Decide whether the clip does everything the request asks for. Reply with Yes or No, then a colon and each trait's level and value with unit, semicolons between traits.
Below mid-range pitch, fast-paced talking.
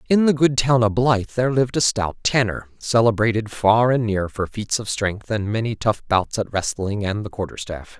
Yes: low, 110 Hz; fast, 210 wpm